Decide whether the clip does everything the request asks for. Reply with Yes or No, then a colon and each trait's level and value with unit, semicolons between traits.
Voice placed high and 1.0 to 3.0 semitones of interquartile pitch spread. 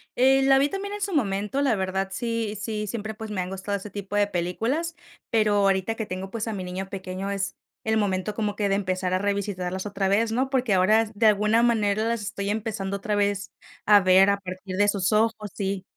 Yes: high, 205 Hz; narrow, 2.5 semitones